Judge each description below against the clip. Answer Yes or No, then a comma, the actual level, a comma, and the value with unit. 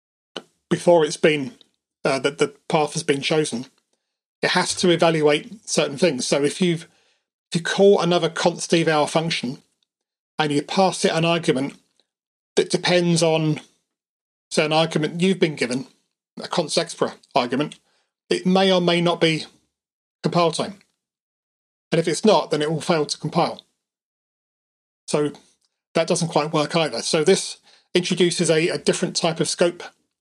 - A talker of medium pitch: Yes, medium, 165 Hz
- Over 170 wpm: No, average, 155 wpm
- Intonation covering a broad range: No, narrow, 2.6 semitones